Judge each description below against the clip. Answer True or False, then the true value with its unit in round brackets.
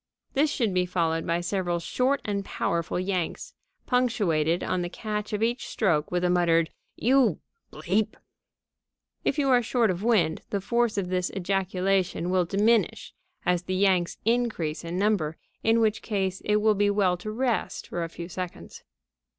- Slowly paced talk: False (165 wpm)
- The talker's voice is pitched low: False (190 Hz)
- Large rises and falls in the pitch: False (3.9 semitones)